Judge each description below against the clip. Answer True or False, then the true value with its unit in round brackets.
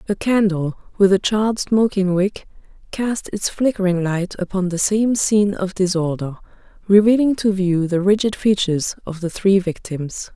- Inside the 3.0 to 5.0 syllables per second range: True (4.8 syllables/s)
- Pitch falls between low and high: False (195 Hz)